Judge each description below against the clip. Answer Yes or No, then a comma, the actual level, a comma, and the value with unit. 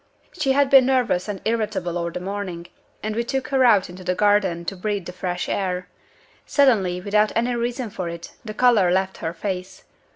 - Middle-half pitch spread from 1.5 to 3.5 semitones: No, average, 4.5 semitones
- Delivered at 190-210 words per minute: Yes, average, 195 wpm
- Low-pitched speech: No, high, 200 Hz